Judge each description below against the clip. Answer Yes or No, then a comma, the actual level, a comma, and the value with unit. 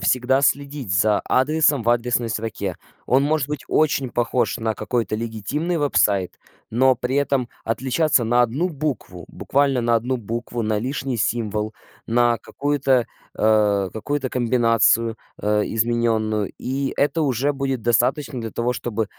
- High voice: No, low, 120 Hz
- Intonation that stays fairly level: No, average, 3.5 semitones